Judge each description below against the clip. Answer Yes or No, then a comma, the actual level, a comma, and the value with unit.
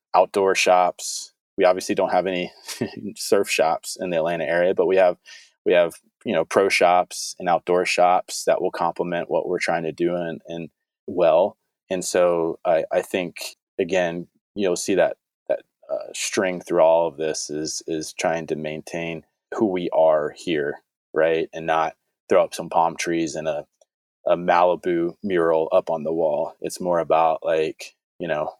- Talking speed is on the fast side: No, average, 175 wpm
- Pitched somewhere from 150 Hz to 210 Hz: No, very low, 85 Hz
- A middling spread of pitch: No, narrow, 1.8 semitones